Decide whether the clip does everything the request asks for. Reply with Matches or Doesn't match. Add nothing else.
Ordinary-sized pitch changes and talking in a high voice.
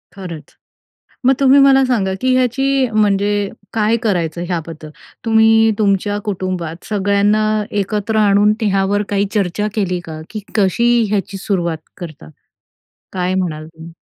Matches